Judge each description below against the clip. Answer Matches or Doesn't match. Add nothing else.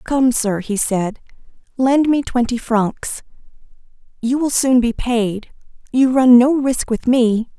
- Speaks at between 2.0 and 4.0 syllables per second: Matches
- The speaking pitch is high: Matches